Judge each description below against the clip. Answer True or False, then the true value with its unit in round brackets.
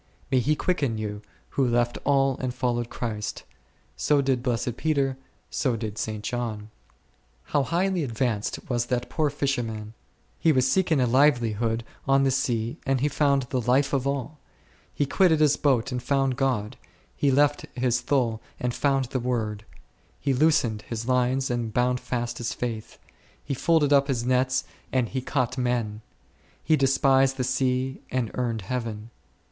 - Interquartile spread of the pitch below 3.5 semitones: True (2.7 semitones)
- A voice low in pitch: True (125 Hz)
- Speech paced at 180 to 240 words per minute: False (165 wpm)